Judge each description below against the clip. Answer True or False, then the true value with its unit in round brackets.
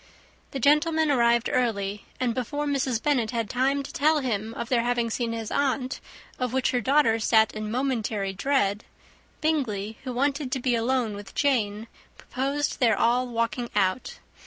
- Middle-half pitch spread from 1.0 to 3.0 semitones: False (3.6 semitones)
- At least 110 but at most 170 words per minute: True (165 wpm)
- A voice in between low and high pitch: False (245 Hz)